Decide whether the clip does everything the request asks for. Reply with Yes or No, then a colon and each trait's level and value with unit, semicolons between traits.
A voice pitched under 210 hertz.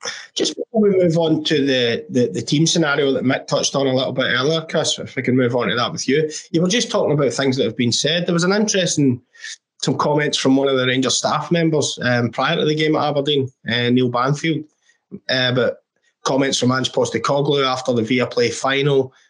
Yes: medium, 140 Hz